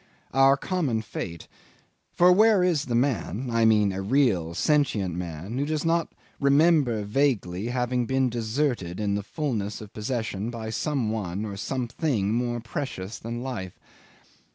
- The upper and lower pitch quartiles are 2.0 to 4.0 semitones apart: No, average, 5.2 semitones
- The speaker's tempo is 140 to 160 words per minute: Yes, average, 150 wpm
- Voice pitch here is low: Yes, low, 120 Hz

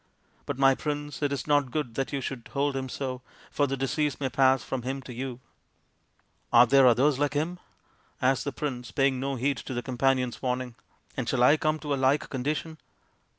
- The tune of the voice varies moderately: No, narrow, 2.1 semitones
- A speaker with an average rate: No, fast, 220 wpm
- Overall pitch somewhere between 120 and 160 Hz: Yes, low, 135 Hz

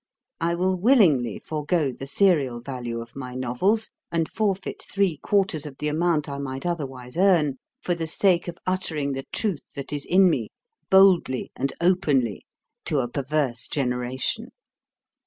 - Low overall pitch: No, medium, 150 Hz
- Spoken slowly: No, average, 155 wpm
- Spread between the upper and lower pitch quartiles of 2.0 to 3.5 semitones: No, wide, 5.6 semitones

